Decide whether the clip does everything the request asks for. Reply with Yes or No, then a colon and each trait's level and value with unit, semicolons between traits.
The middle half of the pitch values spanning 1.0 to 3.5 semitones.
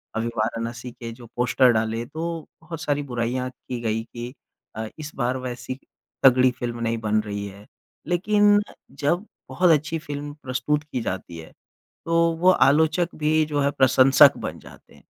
No: average, 4.8 semitones